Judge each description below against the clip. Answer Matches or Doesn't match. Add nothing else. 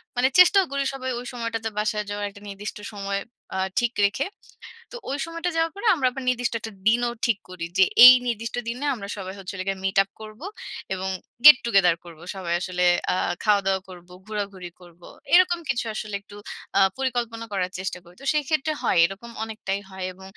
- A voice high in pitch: Matches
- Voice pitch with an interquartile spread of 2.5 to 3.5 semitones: Doesn't match